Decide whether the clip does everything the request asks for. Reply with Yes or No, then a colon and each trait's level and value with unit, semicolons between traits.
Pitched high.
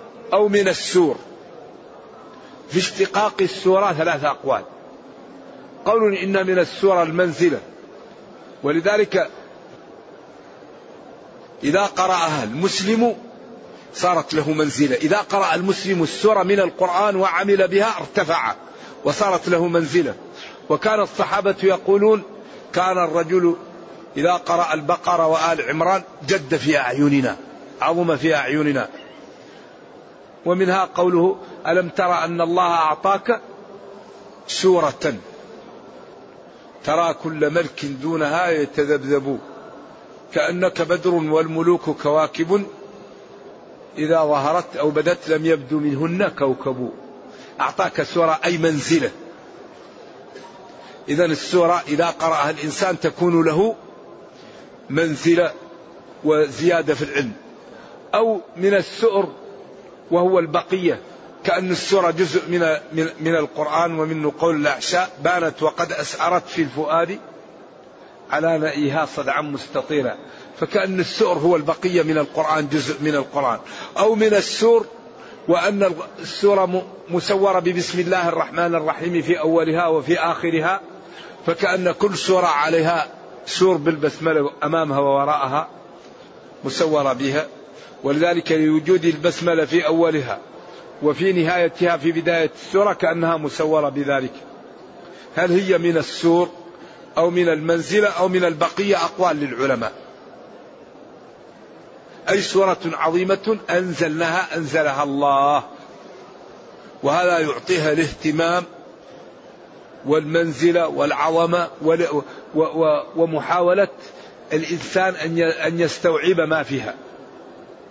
No: medium, 170 Hz